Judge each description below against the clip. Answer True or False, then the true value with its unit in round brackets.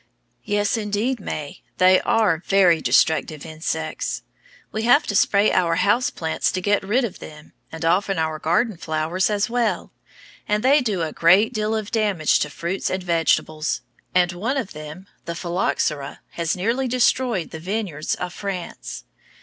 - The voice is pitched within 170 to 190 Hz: True (185 Hz)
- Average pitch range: True (4.7 semitones)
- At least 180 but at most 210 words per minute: False (160 wpm)